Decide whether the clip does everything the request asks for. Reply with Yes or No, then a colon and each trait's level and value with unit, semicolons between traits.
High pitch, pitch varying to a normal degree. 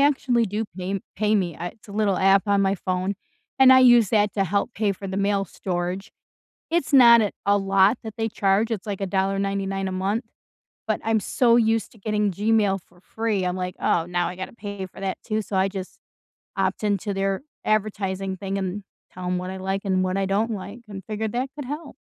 No: high, 200 Hz; narrow, 2.3 semitones